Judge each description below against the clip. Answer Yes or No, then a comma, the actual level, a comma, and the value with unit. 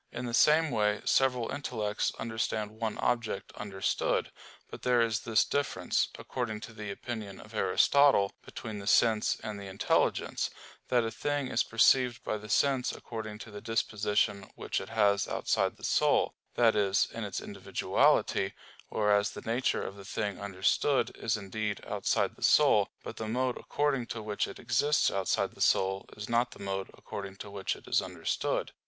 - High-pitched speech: No, low, 110 Hz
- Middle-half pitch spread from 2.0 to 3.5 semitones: Yes, average, 2.9 semitones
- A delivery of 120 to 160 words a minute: No, average, 170 wpm